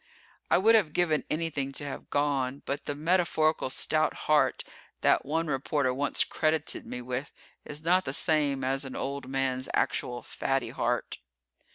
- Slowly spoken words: No, average, 160 wpm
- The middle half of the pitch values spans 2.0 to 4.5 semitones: Yes, average, 2.7 semitones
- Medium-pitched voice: Yes, medium, 145 Hz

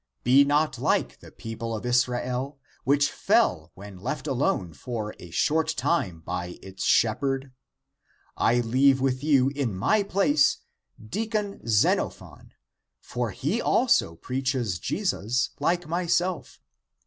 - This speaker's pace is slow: Yes, slow, 130 wpm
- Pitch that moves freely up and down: No, average, 5.0 semitones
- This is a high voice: No, low, 130 Hz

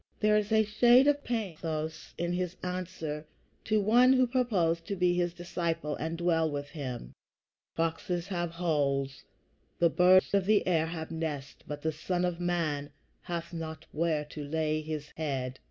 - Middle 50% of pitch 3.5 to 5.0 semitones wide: No, average, 3.0 semitones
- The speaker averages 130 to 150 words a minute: No, average, 165 wpm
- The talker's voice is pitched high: No, medium, 170 Hz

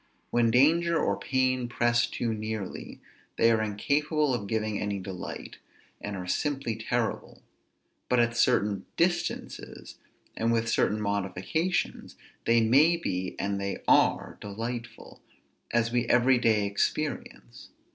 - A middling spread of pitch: Yes, average, 3.9 semitones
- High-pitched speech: No, low, 115 Hz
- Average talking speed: No, slow, 125 wpm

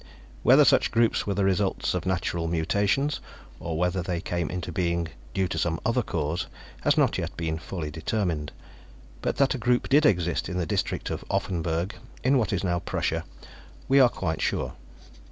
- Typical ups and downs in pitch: Yes, average, 3.7 semitones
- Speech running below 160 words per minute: No, average, 180 wpm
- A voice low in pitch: Yes, very low, 90 Hz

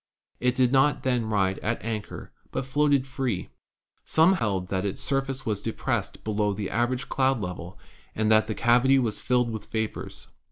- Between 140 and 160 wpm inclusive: No, average, 170 wpm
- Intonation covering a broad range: No, average, 3.9 semitones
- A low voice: Yes, low, 115 Hz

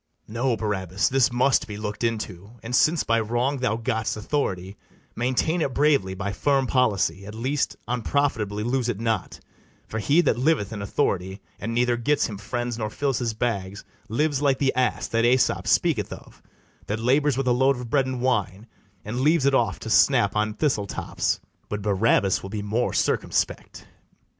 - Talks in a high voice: No, low, 115 Hz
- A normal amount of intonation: Yes, average, 4.1 semitones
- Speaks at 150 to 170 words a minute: No, average, 180 wpm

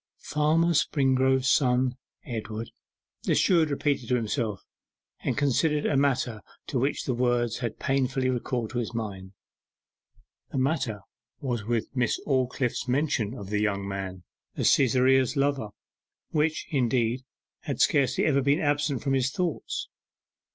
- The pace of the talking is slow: Yes, slow, 130 wpm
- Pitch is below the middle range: Yes, low, 130 Hz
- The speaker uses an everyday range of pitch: Yes, average, 3.3 semitones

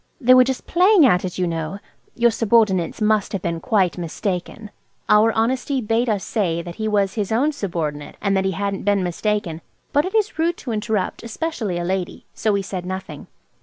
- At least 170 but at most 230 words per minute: Yes, average, 200 wpm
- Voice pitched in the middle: No, high, 205 Hz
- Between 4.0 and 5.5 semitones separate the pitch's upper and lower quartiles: Yes, average, 4.3 semitones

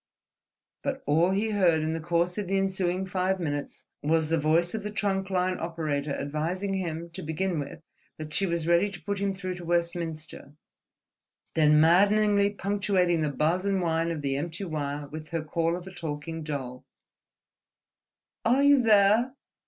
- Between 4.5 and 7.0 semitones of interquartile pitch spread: No, average, 3.7 semitones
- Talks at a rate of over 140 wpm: Yes, average, 170 wpm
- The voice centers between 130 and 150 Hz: No, medium, 170 Hz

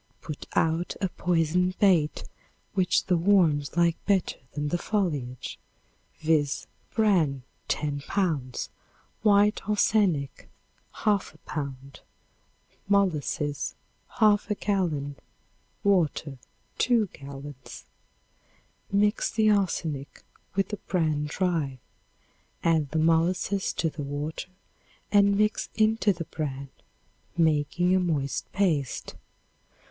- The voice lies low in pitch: No, medium, 165 Hz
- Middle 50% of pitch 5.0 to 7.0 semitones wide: Yes, average, 5.3 semitones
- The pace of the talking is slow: Yes, slow, 100 wpm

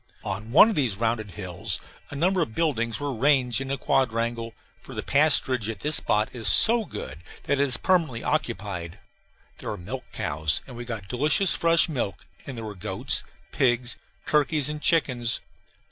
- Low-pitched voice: Yes, low, 125 Hz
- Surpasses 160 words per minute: Yes, average, 175 wpm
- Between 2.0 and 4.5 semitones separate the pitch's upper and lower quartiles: No, average, 5.1 semitones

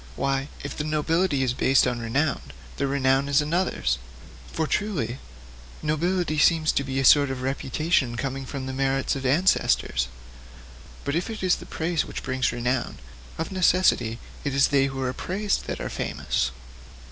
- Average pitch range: Yes, average, 3.5 semitones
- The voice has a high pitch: No, medium, 140 Hz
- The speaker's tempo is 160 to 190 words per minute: Yes, average, 170 wpm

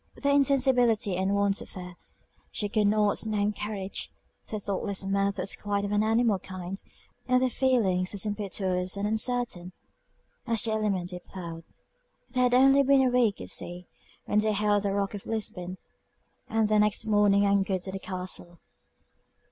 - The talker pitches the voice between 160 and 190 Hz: No, high, 205 Hz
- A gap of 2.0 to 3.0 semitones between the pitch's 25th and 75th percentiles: Yes, narrow, 2.6 semitones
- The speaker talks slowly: No, average, 170 wpm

